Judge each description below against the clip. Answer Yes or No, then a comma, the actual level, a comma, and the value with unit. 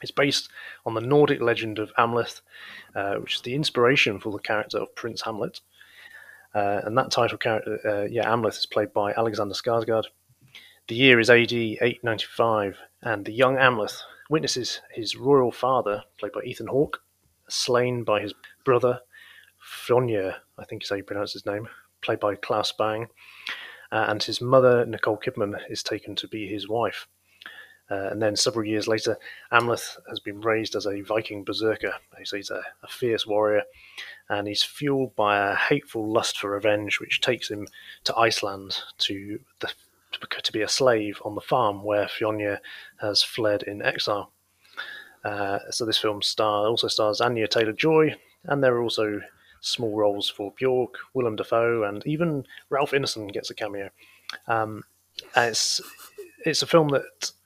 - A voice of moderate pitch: No, low, 110 Hz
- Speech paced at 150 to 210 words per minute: Yes, average, 165 wpm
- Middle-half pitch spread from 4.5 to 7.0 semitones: No, average, 3.0 semitones